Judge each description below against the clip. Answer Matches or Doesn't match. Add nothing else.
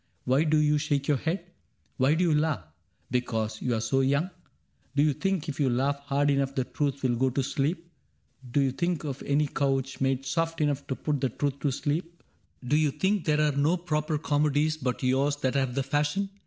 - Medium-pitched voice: Matches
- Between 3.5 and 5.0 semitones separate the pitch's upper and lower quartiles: Doesn't match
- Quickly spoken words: Matches